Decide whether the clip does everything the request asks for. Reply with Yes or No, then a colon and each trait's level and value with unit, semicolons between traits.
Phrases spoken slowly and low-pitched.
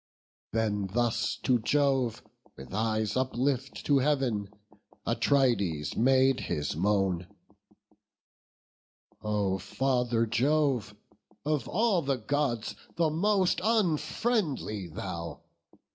Yes: slow, 90 wpm; low, 125 Hz